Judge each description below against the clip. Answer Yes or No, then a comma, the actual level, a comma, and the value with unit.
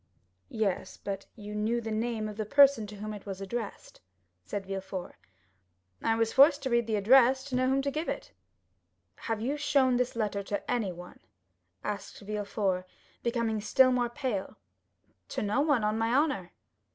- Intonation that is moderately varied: Yes, average, 3.9 semitones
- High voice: Yes, high, 225 Hz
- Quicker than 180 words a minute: No, average, 175 wpm